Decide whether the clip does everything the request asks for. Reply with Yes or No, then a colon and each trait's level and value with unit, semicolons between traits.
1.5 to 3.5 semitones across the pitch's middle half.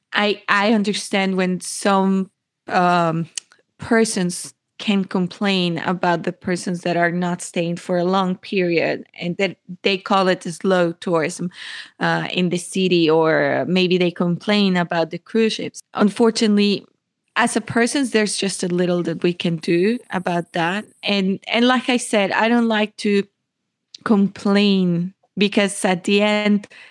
Yes: average, 2.9 semitones